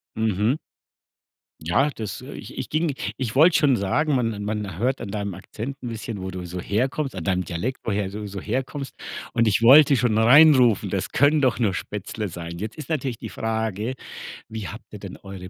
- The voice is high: No, low, 110 Hz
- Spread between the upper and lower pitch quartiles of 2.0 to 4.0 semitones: No, average, 4.8 semitones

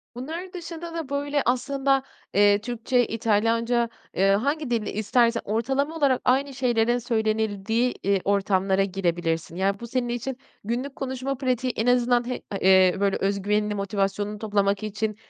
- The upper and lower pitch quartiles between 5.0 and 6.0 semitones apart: No, average, 4.3 semitones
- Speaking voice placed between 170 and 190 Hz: No, high, 230 Hz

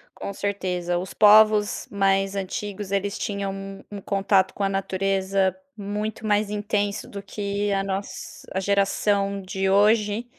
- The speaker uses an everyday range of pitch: No, narrow, 1.1 semitones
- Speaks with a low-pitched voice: No, high, 200 Hz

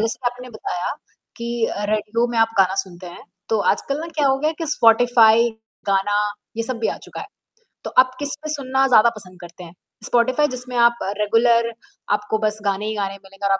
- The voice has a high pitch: Yes, high, 225 Hz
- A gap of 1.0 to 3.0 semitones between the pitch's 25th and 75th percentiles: No, average, 3.5 semitones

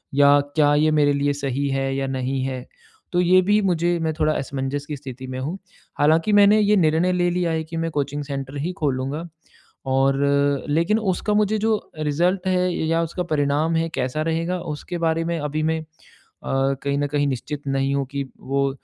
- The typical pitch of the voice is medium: Yes, medium, 150 Hz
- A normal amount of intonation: Yes, average, 3.6 semitones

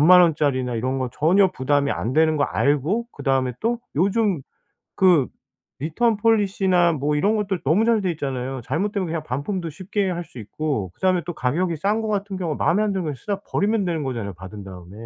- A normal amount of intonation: No, wide, 6.5 semitones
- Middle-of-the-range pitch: Yes, medium, 165 Hz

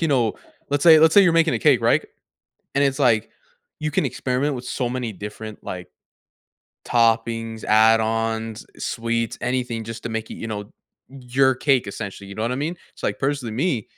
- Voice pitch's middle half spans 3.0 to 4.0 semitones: Yes, average, 3.4 semitones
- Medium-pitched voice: No, low, 120 Hz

